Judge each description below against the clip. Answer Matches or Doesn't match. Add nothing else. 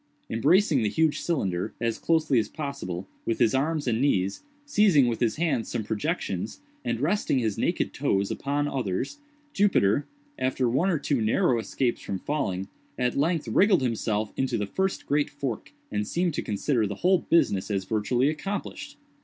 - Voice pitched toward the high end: Doesn't match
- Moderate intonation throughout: Doesn't match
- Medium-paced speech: Matches